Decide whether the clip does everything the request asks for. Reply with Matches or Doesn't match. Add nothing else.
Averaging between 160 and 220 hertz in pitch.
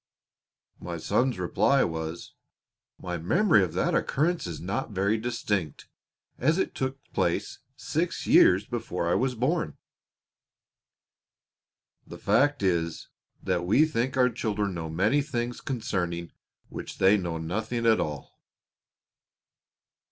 Doesn't match